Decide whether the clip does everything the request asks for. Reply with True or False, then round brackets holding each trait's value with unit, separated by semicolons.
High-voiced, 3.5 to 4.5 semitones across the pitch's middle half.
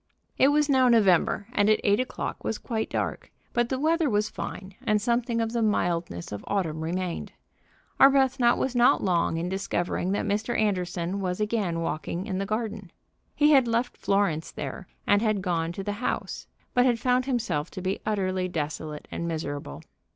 False (205 Hz; 5.2 semitones)